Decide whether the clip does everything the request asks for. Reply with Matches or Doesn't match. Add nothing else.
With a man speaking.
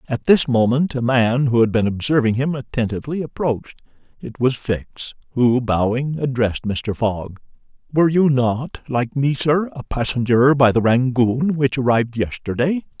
Matches